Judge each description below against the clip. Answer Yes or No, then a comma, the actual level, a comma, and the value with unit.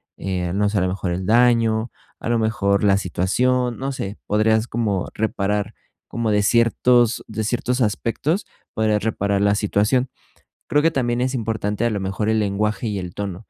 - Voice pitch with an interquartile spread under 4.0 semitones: Yes, average, 2.8 semitones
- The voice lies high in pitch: No, low, 110 Hz